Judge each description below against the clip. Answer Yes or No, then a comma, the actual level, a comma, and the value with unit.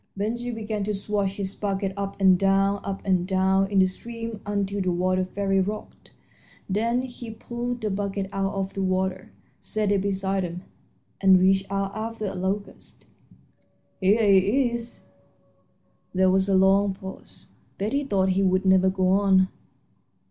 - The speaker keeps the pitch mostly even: Yes, narrow, 1.6 semitones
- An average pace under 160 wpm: No, average, 165 wpm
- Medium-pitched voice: No, high, 195 Hz